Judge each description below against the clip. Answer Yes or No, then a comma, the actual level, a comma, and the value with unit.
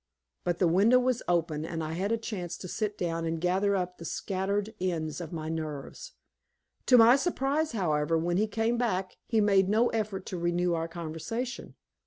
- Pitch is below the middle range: No, medium, 185 Hz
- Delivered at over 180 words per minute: Yes, average, 190 wpm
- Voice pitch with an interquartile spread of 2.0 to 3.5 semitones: No, average, 4.8 semitones